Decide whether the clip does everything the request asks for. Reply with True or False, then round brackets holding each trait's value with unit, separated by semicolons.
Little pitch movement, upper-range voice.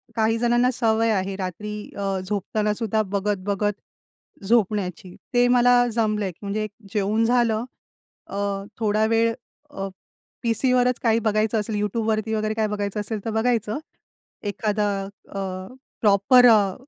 True (2.0 semitones; 215 Hz)